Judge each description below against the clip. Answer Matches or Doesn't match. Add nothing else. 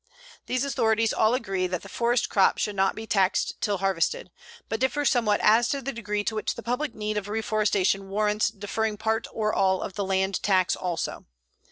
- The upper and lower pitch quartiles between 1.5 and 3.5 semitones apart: Matches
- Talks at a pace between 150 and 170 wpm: Doesn't match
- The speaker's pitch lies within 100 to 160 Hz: Doesn't match